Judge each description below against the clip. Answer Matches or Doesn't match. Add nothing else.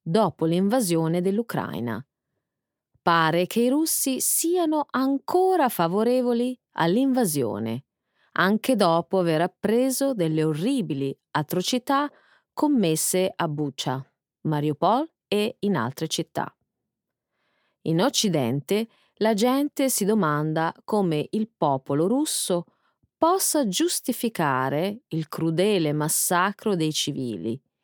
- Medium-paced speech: Doesn't match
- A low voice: Doesn't match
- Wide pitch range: Matches